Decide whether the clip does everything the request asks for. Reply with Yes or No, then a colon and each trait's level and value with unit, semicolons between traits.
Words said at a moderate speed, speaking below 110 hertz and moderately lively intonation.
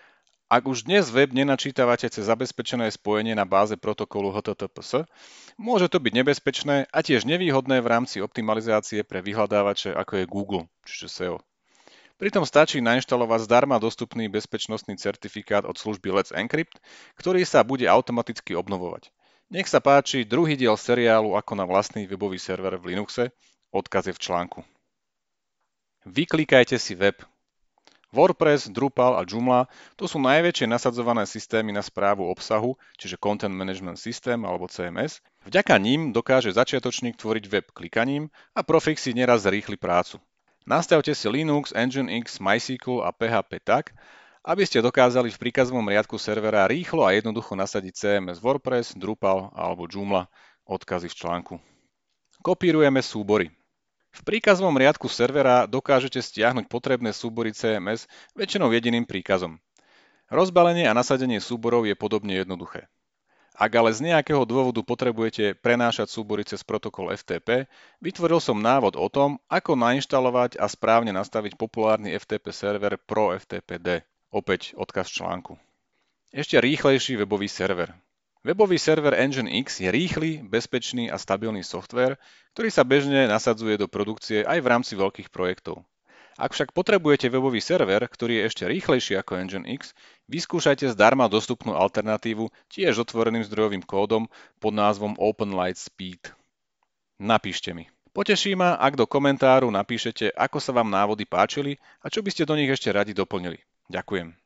No: average, 140 wpm; low, 115 Hz; average, 4.5 semitones